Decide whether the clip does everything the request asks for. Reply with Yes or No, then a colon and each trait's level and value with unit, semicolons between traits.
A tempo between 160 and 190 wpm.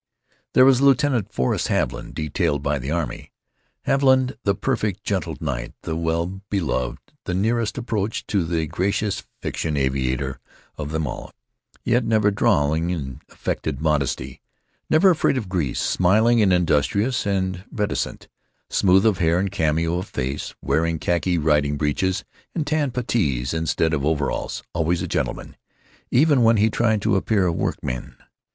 No: average, 145 wpm